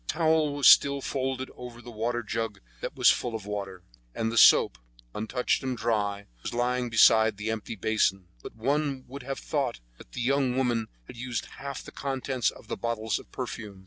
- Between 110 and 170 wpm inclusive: No, average, 190 wpm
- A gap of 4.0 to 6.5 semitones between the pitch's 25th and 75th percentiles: No, average, 3.2 semitones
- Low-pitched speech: Yes, low, 120 Hz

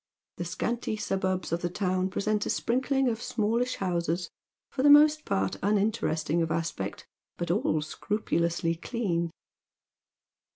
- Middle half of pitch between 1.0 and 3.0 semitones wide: No, average, 5.2 semitones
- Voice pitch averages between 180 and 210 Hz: Yes, medium, 185 Hz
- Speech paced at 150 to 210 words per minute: No, slow, 135 wpm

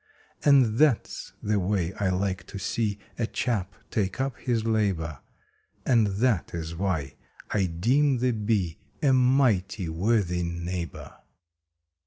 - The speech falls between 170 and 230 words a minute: No, slow, 135 wpm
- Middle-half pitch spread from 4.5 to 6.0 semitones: Yes, average, 4.8 semitones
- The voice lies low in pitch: Yes, low, 100 Hz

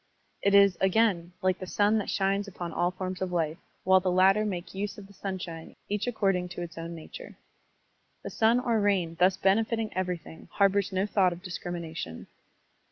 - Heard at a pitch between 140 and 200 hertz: Yes, high, 190 Hz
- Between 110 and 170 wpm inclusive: No, average, 180 wpm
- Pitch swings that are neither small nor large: No, narrow, 2.3 semitones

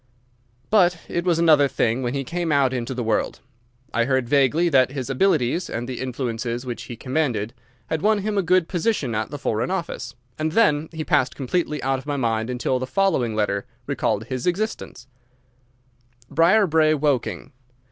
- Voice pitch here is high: No, low, 135 Hz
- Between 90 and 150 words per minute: No, average, 175 wpm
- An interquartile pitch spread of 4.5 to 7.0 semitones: Yes, wide, 5.4 semitones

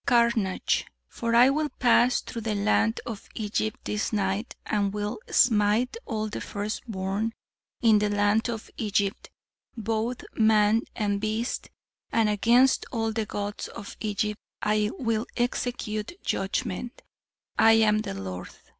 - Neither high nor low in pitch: No, high, 215 Hz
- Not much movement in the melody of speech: Yes, narrow, 1.9 semitones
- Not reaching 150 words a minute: Yes, slow, 135 wpm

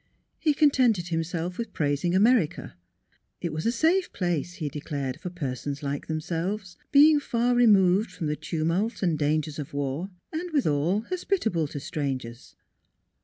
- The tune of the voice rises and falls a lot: Yes, wide, 7.4 semitones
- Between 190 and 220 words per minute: No, average, 145 wpm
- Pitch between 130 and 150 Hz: No, medium, 175 Hz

